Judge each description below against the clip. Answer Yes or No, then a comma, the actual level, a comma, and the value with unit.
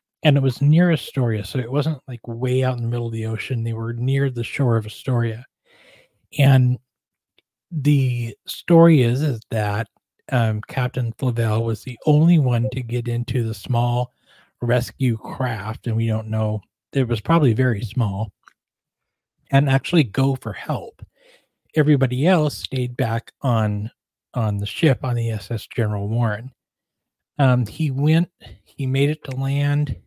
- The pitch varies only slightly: No, average, 3.4 semitones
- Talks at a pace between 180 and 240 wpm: No, average, 160 wpm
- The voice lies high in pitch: No, low, 125 Hz